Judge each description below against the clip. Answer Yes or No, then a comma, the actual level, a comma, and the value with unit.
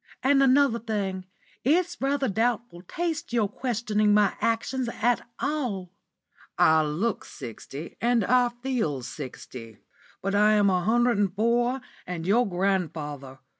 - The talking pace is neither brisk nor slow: No, slow, 130 wpm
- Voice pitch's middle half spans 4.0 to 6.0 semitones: Yes, average, 5.3 semitones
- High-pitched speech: Yes, high, 215 Hz